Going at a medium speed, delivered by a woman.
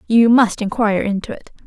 Yes: average, 180 wpm; female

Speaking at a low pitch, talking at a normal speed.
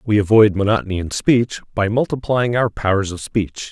Yes: low, 105 Hz; average, 180 wpm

